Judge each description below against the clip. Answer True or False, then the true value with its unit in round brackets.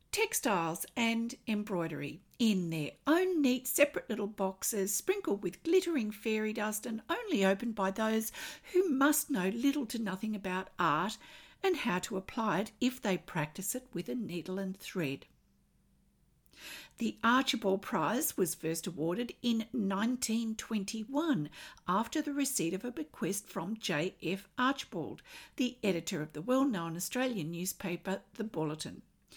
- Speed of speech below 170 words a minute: True (140 wpm)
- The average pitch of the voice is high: True (215 Hz)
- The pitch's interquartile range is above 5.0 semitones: True (5.5 semitones)